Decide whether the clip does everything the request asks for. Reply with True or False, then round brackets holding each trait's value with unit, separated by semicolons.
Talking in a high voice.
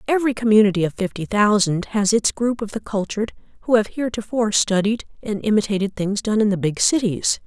True (210 Hz)